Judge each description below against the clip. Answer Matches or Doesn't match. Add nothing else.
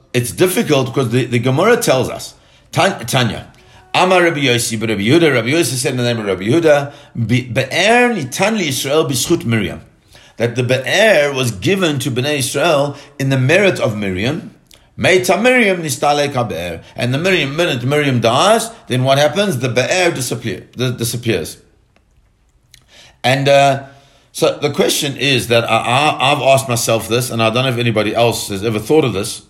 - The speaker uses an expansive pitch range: Doesn't match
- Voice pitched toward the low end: Matches